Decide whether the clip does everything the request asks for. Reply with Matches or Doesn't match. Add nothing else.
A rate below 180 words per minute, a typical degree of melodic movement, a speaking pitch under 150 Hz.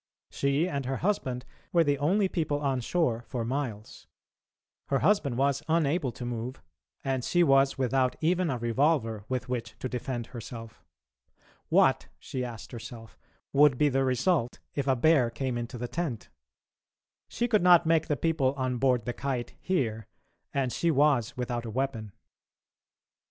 Matches